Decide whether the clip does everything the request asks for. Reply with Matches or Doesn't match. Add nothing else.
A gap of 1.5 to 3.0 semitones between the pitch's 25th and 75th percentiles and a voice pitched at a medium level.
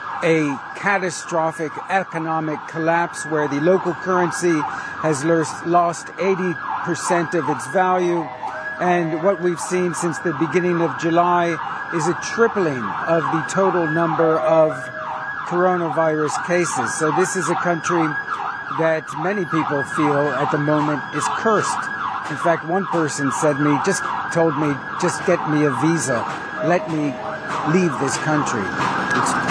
Matches